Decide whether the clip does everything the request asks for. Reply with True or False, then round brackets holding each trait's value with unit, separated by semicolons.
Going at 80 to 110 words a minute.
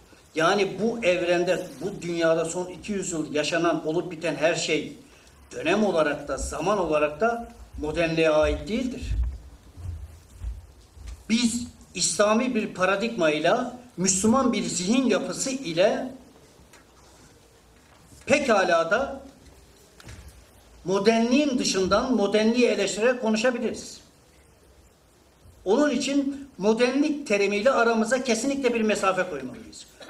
True (95 wpm)